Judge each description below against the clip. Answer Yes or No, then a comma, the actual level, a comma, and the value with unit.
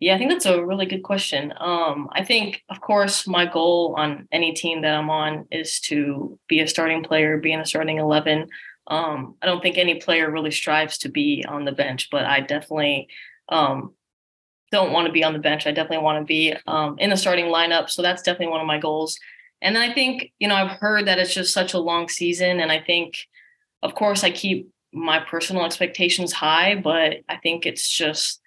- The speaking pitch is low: No, medium, 165 Hz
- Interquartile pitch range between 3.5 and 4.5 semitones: No, average, 3.1 semitones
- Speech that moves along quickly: Yes, fast, 220 wpm